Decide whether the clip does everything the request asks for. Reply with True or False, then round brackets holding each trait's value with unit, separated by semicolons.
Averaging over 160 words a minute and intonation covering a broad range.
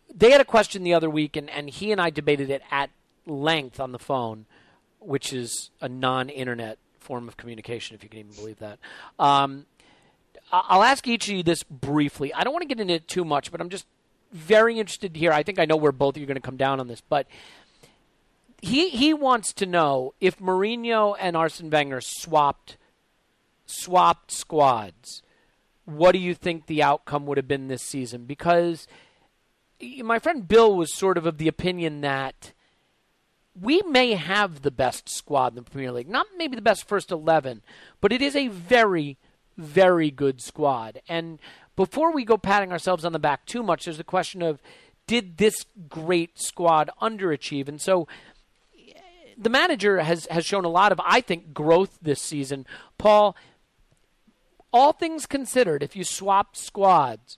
True (185 wpm; 6.4 semitones)